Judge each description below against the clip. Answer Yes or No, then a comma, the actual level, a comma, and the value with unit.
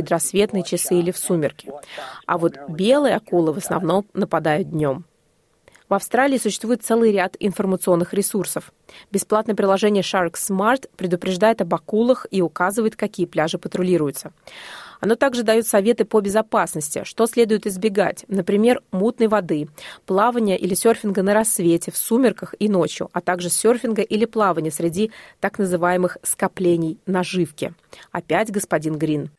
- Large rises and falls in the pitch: No, average, 3.7 semitones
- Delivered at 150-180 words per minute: No, average, 135 wpm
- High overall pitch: Yes, high, 195 Hz